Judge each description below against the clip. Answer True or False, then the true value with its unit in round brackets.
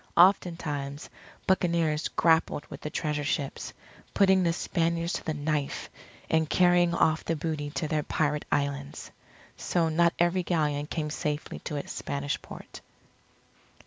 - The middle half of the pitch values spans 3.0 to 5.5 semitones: False (2.6 semitones)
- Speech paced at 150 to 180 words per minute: False (140 wpm)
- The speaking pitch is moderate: True (160 Hz)